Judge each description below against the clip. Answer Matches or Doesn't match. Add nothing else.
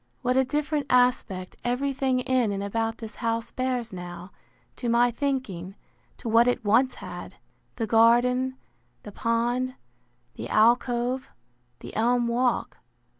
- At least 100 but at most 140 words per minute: Matches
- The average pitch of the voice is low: Doesn't match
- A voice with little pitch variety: Matches